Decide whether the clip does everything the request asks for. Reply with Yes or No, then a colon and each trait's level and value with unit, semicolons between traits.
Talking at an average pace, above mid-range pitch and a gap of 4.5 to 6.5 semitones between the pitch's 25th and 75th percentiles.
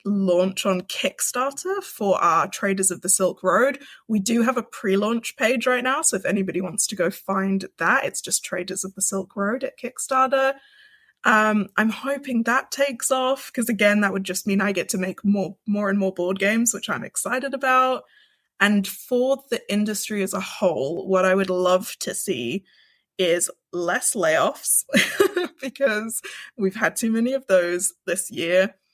Yes: average, 180 wpm; high, 210 Hz; wide, 5.4 semitones